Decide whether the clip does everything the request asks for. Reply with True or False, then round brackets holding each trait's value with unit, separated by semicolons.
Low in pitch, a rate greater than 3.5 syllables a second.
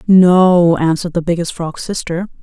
False (170 Hz; 4.6 syllables/s)